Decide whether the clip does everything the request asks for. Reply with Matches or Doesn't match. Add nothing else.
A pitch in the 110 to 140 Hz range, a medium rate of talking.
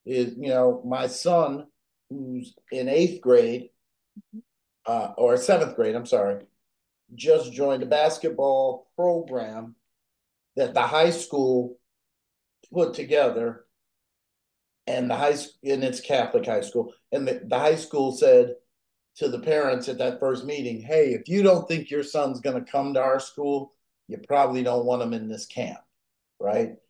Matches